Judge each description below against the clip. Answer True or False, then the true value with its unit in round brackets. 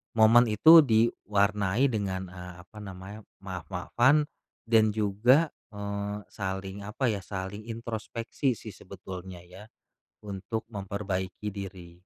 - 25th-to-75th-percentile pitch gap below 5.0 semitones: True (2.9 semitones)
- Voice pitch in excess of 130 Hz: False (100 Hz)